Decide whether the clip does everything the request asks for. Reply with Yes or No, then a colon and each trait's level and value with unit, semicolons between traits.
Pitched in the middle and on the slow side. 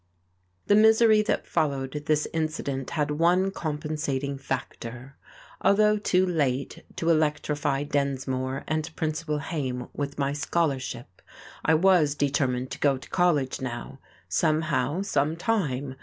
Yes: medium, 145 Hz; slow, 120 wpm